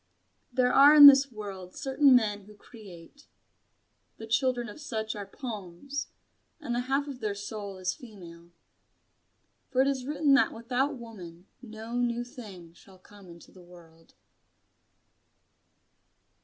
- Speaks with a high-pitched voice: Yes, high, 225 Hz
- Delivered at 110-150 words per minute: Yes, average, 140 wpm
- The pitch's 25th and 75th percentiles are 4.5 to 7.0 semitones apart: Yes, average, 5.3 semitones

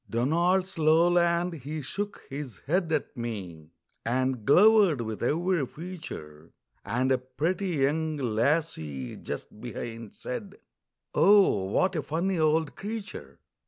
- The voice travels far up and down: Yes, wide, 6.7 semitones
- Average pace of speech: No, slow, 120 wpm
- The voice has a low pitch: No, medium, 155 Hz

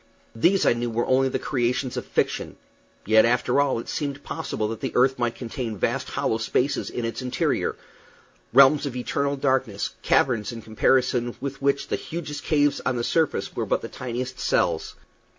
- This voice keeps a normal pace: Yes, average, 180 wpm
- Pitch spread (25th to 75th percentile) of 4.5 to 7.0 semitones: No, average, 2.9 semitones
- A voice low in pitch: Yes, low, 125 Hz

